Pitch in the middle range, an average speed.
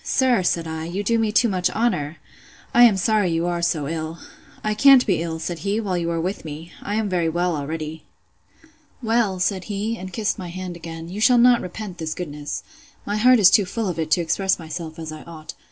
No: medium, 180 Hz; fast, 220 wpm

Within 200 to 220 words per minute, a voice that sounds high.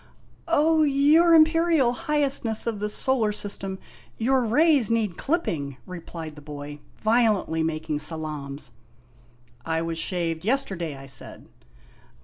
No: slow, 135 wpm; high, 200 Hz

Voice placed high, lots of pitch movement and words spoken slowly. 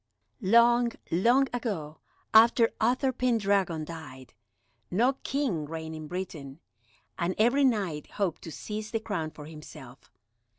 Yes: high, 195 Hz; wide, 6.9 semitones; slow, 125 wpm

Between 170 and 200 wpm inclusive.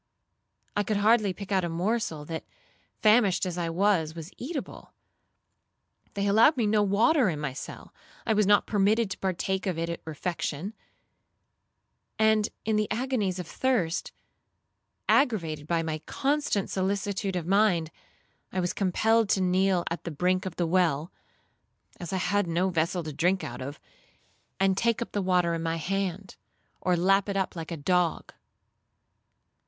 No: average, 160 wpm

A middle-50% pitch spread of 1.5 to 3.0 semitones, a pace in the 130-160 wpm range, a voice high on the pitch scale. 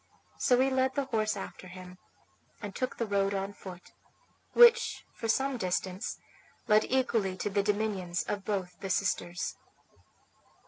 No: average, 4.5 semitones; average, 145 wpm; high, 205 Hz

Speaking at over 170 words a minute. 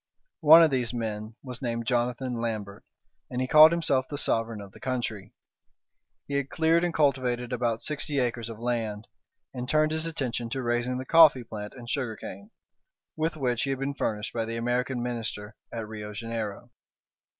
Yes: average, 180 wpm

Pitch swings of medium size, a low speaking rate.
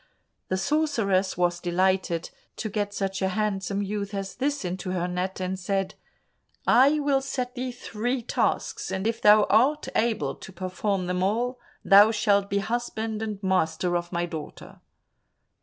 No: average, 3.8 semitones; average, 155 wpm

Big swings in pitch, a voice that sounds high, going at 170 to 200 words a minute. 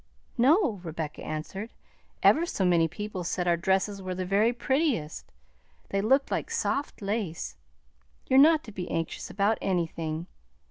No: wide, 5.7 semitones; high, 195 Hz; average, 145 wpm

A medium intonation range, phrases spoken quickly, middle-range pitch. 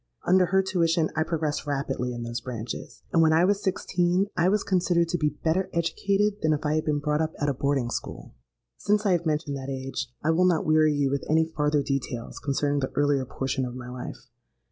Yes: average, 4.0 semitones; fast, 220 wpm; medium, 155 Hz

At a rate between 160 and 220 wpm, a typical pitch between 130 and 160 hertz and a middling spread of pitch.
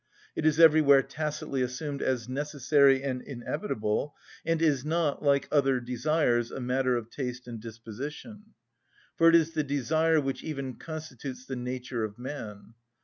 No: average, 150 wpm; low, 135 Hz; average, 3.5 semitones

